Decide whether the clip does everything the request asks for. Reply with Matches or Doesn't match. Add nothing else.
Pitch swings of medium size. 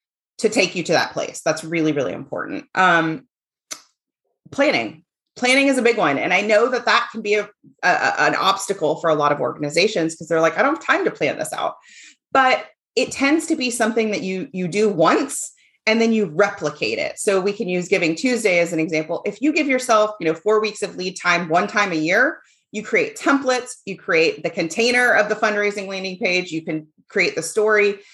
Doesn't match